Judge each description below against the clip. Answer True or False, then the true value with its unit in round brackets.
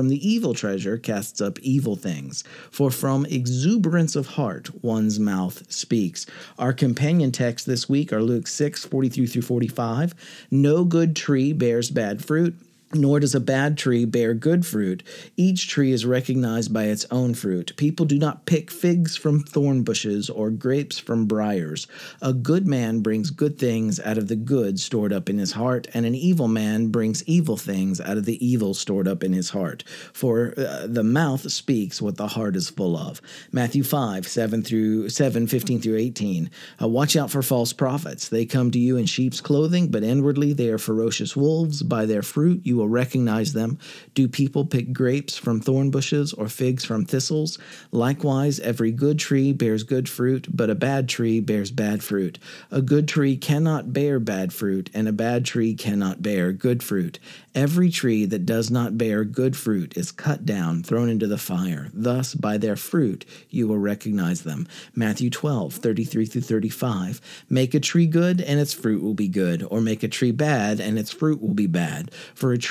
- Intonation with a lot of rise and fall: False (4.7 semitones)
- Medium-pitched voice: False (125 Hz)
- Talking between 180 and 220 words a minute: True (190 wpm)